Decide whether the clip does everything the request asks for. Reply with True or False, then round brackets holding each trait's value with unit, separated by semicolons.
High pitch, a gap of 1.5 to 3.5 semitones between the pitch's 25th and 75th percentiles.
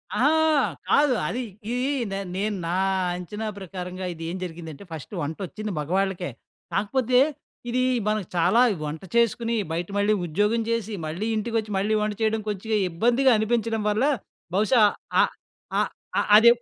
False (210 Hz; 4.0 semitones)